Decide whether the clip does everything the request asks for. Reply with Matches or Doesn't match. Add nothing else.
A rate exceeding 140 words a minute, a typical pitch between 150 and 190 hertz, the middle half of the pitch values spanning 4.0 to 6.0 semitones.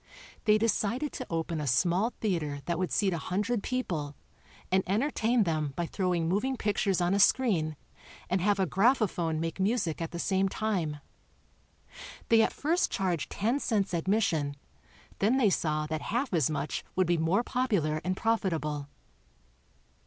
Matches